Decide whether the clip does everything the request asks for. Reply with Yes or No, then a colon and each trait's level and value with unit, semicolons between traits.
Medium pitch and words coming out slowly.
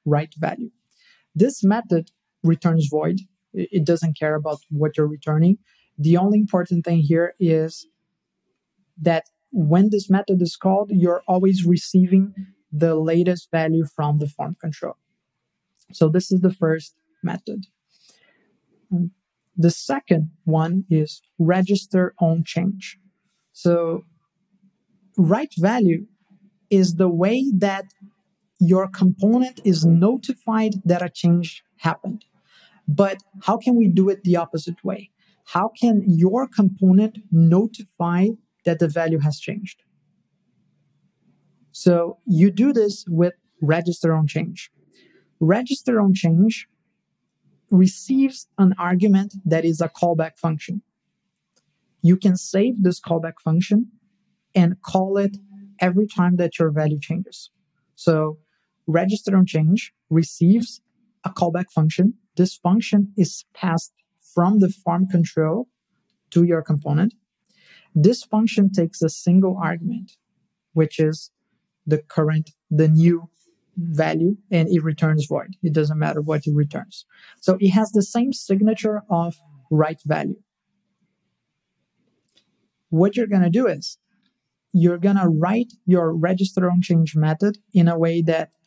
Yes: medium, 180 Hz; slow, 125 wpm